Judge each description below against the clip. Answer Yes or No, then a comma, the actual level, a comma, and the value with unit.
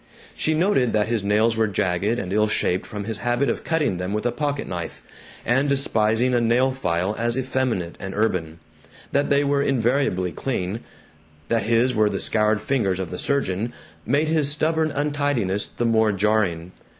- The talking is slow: No, average, 175 wpm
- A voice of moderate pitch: No, low, 115 Hz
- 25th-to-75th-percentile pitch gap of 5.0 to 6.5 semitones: Yes, average, 5.3 semitones